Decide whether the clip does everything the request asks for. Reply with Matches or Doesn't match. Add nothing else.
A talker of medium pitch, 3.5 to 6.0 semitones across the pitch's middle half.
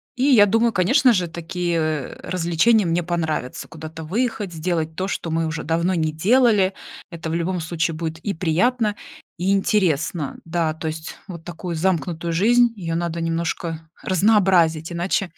Doesn't match